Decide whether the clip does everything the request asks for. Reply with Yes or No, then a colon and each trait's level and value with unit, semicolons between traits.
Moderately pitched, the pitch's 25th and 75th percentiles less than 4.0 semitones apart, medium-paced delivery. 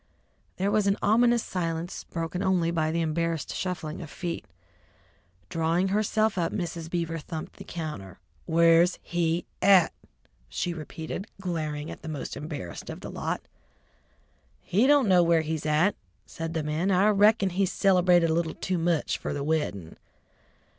Yes: medium, 170 Hz; average, 2.8 semitones; average, 155 wpm